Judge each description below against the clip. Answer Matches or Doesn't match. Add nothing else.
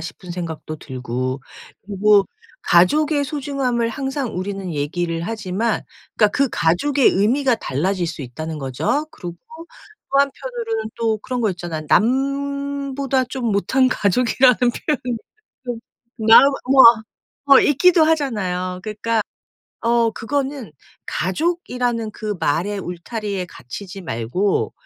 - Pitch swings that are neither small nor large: Doesn't match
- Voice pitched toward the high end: Matches